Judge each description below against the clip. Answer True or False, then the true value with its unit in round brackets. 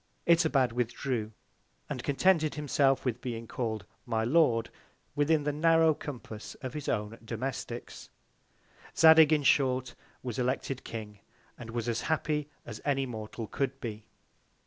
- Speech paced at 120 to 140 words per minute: True (135 wpm)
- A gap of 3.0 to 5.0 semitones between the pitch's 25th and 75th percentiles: True (4.5 semitones)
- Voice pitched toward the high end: False (130 Hz)